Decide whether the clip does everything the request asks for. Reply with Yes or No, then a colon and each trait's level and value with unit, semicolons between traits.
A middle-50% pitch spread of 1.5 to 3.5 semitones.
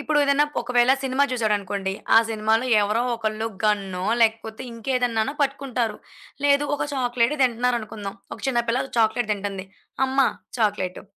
Yes: average, 3.2 semitones